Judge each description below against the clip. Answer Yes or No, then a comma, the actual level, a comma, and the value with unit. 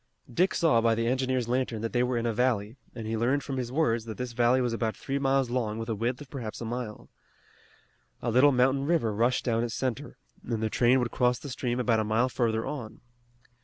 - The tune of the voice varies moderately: No, narrow, 2.2 semitones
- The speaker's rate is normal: No, fast, 240 wpm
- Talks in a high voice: No, low, 120 Hz